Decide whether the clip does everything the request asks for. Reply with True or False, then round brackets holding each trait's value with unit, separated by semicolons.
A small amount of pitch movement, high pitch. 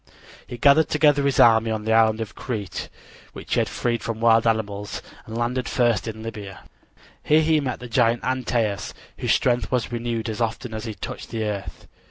False (2.1 semitones; 115 Hz)